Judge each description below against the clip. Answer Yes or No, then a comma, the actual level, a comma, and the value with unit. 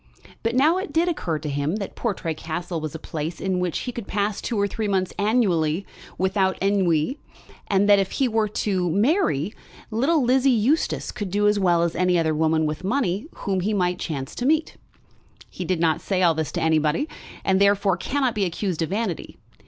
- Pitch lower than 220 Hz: Yes, high, 190 Hz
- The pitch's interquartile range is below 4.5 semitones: No, average, 4.8 semitones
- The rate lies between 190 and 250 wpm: Yes, average, 200 wpm